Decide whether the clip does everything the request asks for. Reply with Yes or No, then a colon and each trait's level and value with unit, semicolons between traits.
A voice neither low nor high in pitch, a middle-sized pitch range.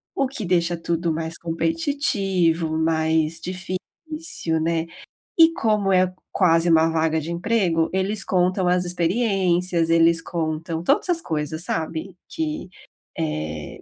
Yes: medium, 170 Hz; average, 3.1 semitones